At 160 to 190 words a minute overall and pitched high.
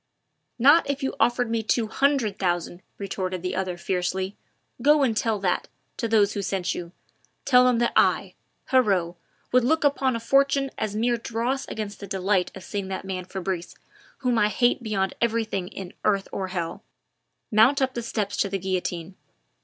Yes: average, 175 wpm; high, 210 Hz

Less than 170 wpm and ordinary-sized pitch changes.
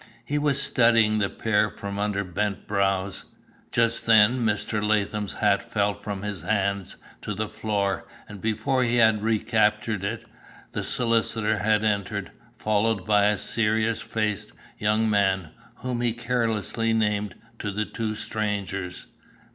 No: average, 140 wpm; narrow, 1.7 semitones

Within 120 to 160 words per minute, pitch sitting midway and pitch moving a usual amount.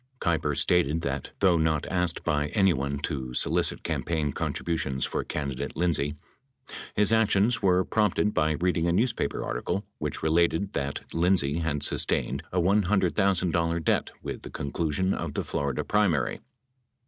No: average, 145 wpm; very low, 85 Hz; average, 4.4 semitones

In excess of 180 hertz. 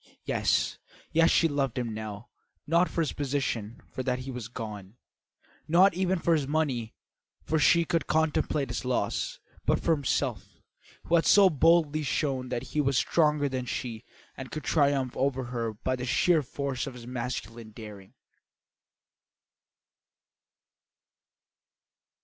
No: low, 135 Hz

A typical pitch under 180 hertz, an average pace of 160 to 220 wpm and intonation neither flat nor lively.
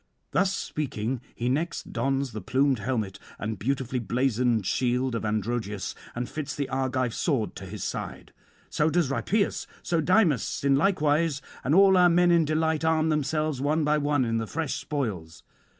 Yes: low, 135 Hz; average, 170 wpm; average, 4.7 semitones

